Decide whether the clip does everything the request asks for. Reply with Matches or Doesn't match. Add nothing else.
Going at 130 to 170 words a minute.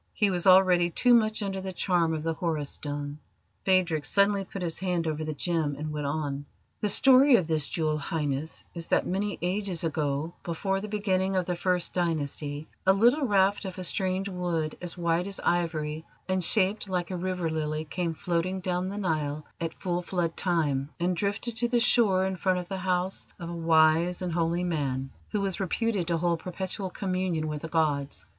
Doesn't match